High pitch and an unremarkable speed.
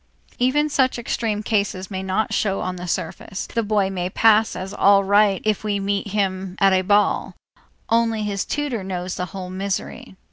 Yes: high, 200 Hz; average, 180 wpm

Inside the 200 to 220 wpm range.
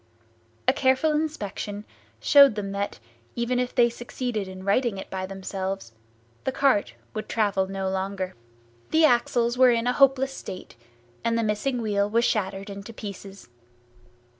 No: average, 150 wpm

